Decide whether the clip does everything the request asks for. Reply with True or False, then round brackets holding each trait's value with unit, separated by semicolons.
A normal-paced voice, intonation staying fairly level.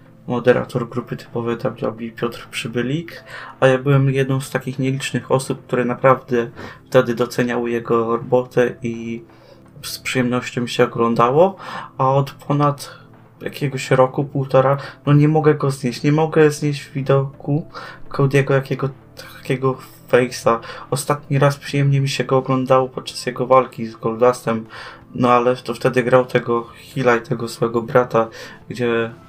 True (145 wpm; 2.2 semitones)